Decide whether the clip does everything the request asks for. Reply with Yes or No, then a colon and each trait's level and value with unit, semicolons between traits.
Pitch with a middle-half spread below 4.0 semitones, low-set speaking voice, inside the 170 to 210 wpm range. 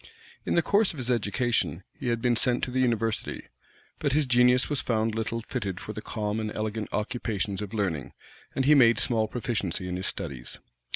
Yes: average, 3.0 semitones; low, 115 Hz; average, 195 wpm